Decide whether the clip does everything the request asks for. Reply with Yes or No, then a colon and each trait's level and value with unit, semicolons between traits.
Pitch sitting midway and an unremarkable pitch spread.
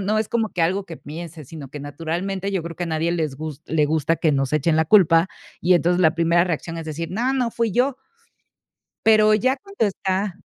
Yes: medium, 170 Hz; average, 4.0 semitones